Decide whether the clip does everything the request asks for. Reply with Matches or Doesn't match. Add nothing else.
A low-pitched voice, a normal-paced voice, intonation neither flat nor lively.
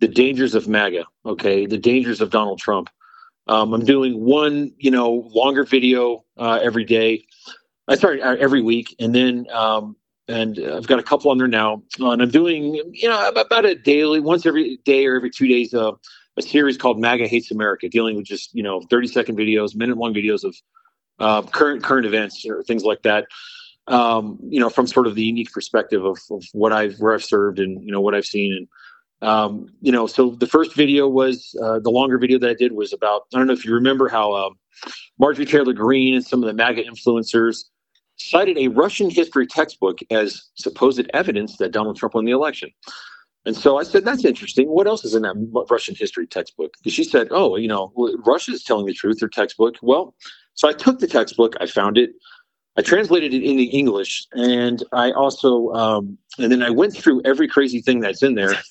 Doesn't match